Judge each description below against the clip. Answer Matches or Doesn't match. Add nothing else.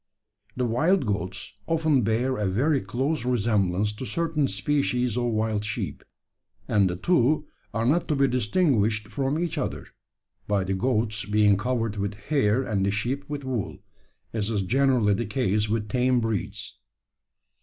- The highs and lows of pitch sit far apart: Doesn't match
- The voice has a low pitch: Matches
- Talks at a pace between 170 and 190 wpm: Doesn't match